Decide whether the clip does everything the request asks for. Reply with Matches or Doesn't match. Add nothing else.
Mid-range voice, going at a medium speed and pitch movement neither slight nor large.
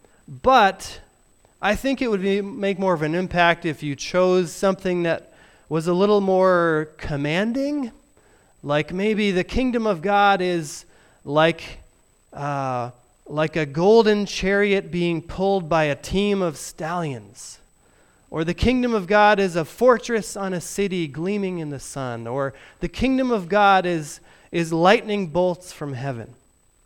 Matches